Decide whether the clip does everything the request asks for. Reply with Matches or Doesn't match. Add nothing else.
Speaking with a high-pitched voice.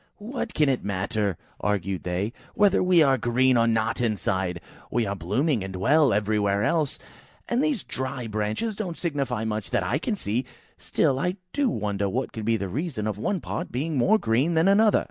Doesn't match